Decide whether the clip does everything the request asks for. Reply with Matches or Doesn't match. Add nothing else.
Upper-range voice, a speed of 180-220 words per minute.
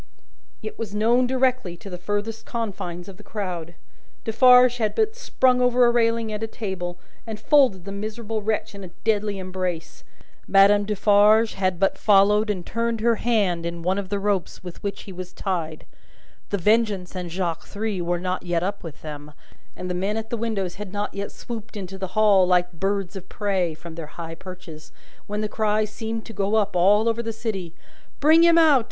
Matches